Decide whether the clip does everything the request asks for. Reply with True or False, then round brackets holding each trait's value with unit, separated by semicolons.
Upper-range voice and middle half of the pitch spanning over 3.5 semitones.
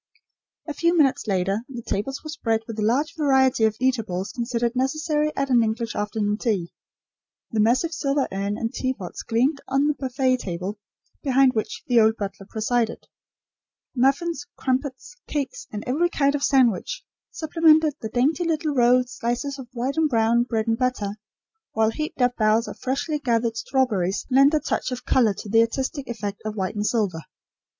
True (250 Hz; 4.1 semitones)